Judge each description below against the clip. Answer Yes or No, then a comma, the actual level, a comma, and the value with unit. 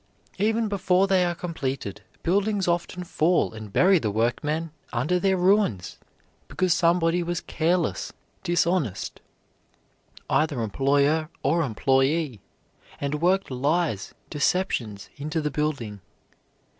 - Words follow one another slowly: Yes, slow, 110 wpm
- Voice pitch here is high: No, medium, 160 Hz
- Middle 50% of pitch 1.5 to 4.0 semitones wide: No, average, 5.0 semitones